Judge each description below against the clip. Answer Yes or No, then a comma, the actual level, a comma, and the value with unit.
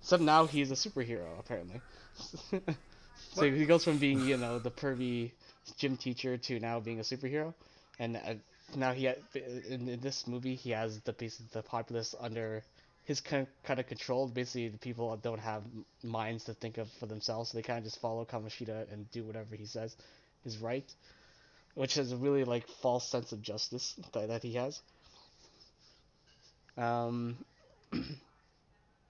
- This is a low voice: Yes, low, 120 Hz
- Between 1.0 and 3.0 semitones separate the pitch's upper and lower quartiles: Yes, average, 2.7 semitones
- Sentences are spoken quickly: No, average, 170 wpm